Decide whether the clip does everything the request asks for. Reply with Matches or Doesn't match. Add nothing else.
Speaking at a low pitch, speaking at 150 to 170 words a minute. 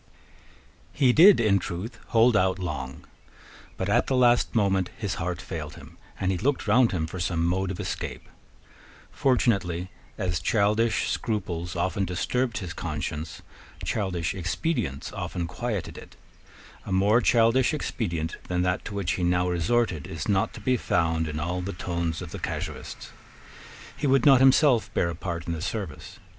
Matches